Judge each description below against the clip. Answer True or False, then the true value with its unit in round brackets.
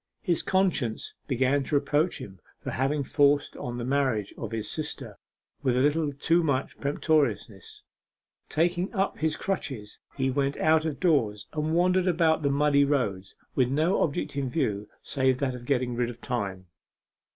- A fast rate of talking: False (165 wpm)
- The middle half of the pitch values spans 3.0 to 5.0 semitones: True (4.2 semitones)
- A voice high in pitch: False (140 Hz)